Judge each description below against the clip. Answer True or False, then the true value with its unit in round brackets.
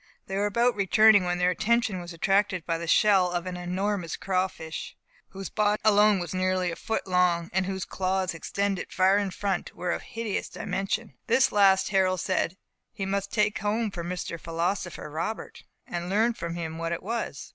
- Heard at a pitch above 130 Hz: True (190 Hz)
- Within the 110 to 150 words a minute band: False (185 wpm)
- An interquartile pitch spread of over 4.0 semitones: False (2.6 semitones)